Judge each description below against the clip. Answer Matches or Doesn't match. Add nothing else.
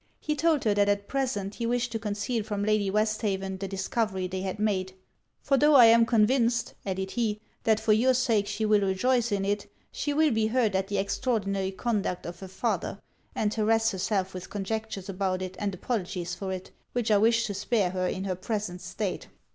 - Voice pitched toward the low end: Doesn't match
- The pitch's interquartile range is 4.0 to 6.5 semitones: Doesn't match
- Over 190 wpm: Matches